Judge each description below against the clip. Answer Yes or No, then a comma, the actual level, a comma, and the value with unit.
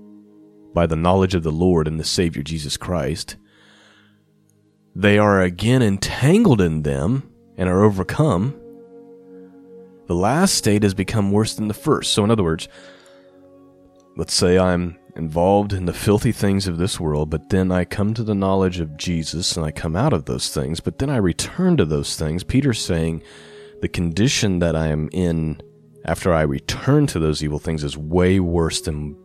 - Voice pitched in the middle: No, very low, 95 Hz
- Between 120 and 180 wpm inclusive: Yes, average, 175 wpm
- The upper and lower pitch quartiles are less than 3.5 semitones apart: No, average, 4.0 semitones